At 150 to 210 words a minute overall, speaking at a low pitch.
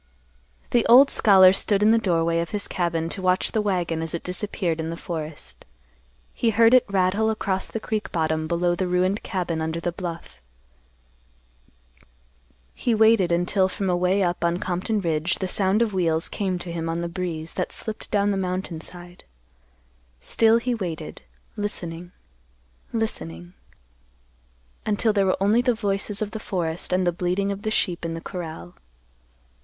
No: average, 170 wpm; medium, 185 Hz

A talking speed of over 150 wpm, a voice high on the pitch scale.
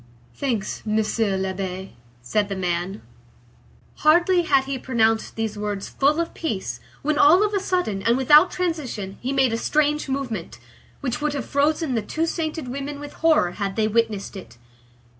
Yes: average, 165 wpm; very high, 255 Hz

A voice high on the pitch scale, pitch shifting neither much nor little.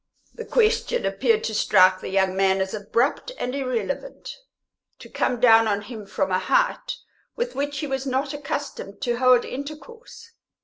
No: very high, 255 Hz; wide, 6.9 semitones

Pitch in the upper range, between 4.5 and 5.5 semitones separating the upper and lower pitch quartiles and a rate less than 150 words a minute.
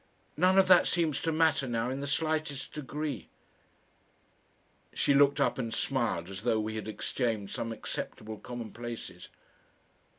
No: low, 130 Hz; average, 5.2 semitones; average, 140 wpm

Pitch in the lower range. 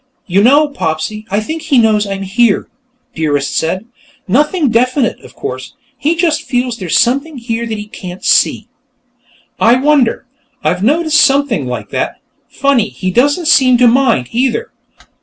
No: high, 240 Hz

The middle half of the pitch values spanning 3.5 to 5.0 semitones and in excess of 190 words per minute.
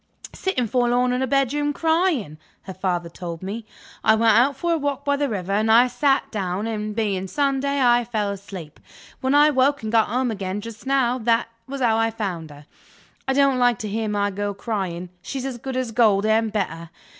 Yes: average, 4.6 semitones; fast, 205 wpm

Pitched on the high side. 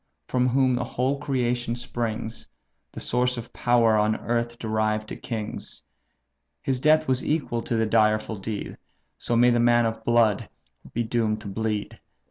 No: low, 120 Hz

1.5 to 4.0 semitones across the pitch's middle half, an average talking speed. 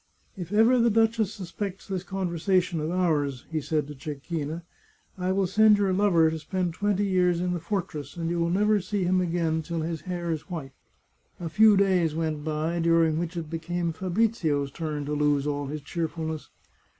Yes: average, 3.1 semitones; average, 195 wpm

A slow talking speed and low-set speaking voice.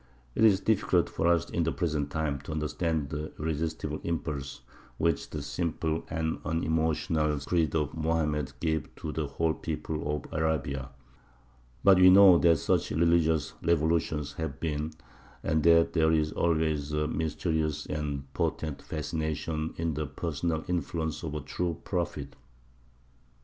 No: average, 145 wpm; very low, 80 Hz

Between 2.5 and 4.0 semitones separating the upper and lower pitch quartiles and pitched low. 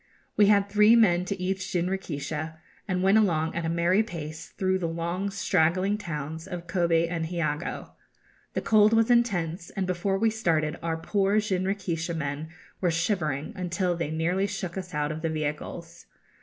No: average, 3.2 semitones; medium, 175 Hz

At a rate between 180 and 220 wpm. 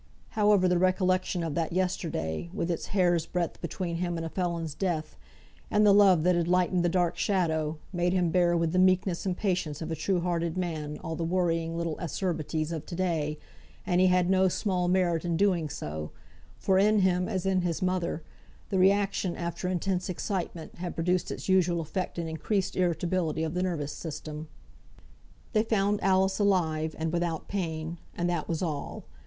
Yes: average, 185 wpm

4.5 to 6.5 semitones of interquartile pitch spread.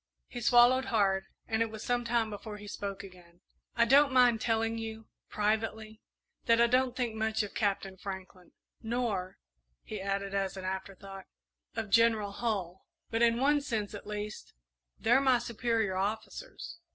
No: average, 3.0 semitones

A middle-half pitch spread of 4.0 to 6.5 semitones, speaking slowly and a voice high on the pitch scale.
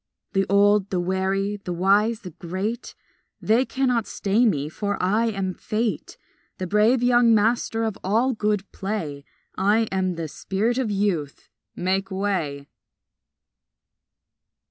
No: average, 3.0 semitones; slow, 130 wpm; high, 200 Hz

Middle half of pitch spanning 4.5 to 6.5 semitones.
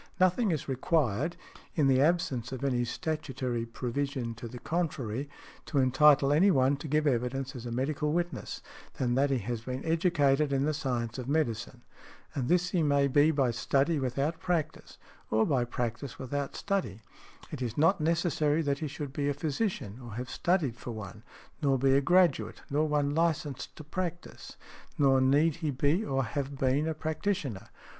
No: average, 3.6 semitones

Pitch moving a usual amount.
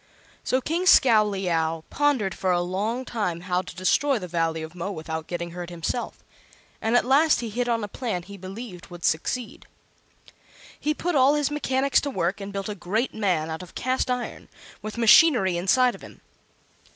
No: wide, 6.3 semitones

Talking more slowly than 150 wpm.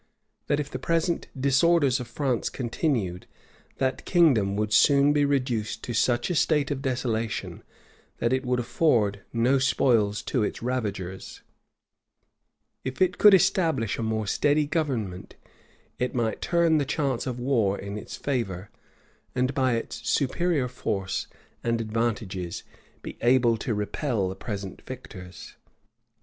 Yes: average, 140 wpm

